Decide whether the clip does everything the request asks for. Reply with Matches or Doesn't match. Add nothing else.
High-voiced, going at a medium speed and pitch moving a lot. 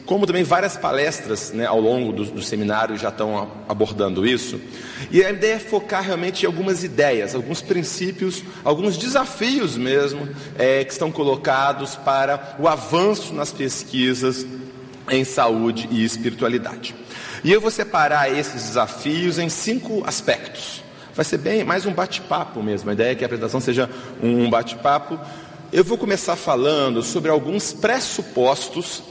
Doesn't match